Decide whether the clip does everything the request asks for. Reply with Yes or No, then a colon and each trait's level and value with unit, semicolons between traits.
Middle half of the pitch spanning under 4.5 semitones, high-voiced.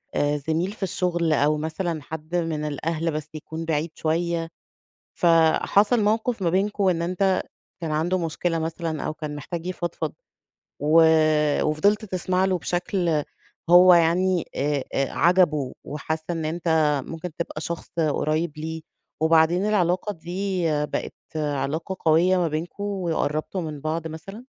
No: average, 2.7 semitones; medium, 165 Hz